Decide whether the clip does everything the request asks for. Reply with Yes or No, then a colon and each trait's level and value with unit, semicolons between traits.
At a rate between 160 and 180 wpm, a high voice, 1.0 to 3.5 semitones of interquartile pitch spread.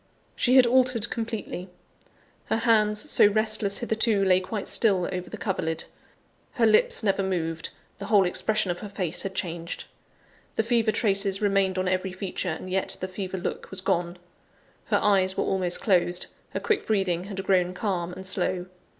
Yes: average, 170 wpm; high, 195 Hz; average, 2.8 semitones